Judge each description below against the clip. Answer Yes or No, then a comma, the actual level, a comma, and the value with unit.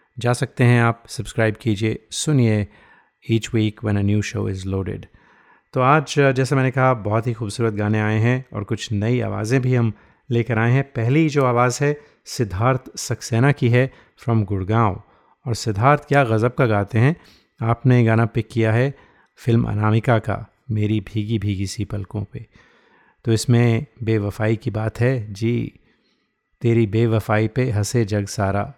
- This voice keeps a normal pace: Yes, average, 165 wpm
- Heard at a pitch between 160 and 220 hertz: No, low, 115 Hz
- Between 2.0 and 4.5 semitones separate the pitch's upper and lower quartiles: Yes, average, 2.7 semitones